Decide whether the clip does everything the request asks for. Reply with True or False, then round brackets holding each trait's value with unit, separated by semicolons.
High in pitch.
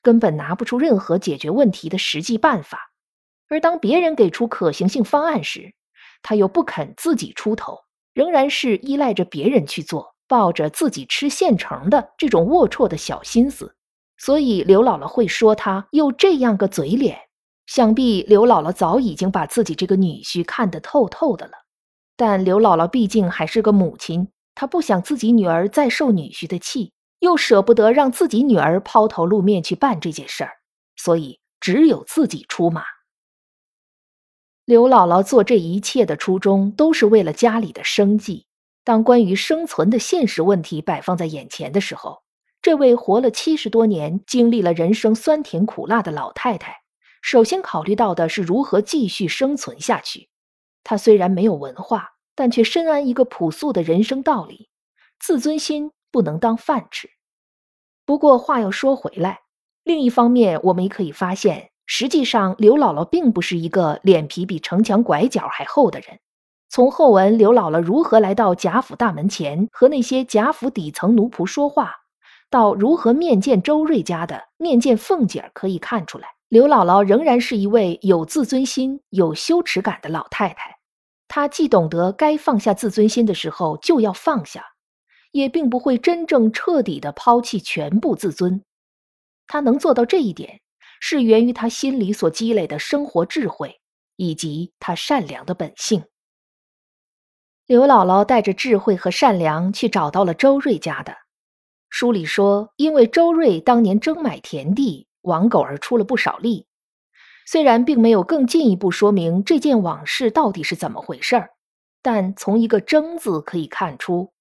True (220 Hz)